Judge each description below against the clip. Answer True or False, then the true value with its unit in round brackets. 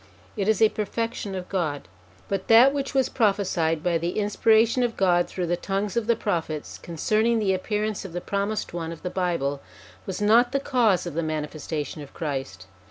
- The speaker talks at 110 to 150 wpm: False (195 wpm)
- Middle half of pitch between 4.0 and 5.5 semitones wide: True (4.6 semitones)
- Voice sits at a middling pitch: False (195 Hz)